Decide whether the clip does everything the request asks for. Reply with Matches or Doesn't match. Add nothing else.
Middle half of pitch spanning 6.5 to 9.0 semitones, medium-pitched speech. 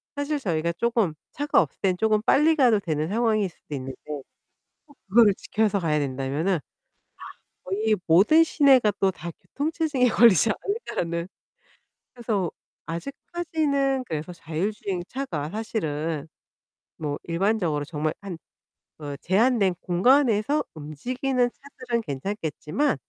Doesn't match